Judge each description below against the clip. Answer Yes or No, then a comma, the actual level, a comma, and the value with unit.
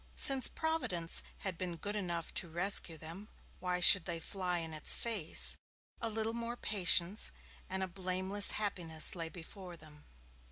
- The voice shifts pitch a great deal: No, average, 3.4 semitones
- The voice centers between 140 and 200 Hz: Yes, medium, 185 Hz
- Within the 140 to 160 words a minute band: Yes, average, 150 wpm